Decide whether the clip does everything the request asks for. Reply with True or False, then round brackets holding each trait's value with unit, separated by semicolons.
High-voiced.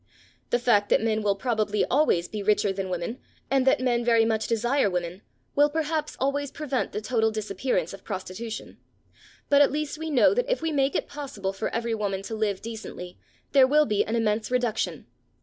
True (230 Hz)